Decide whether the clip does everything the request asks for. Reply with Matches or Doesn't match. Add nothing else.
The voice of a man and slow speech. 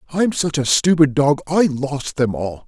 Doesn't match